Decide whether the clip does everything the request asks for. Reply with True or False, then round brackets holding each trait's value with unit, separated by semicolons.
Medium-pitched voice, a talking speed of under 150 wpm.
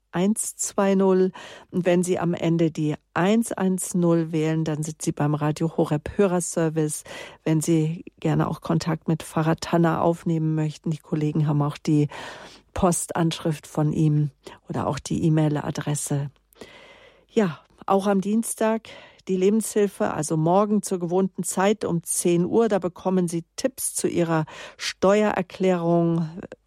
True (170 Hz; 135 wpm)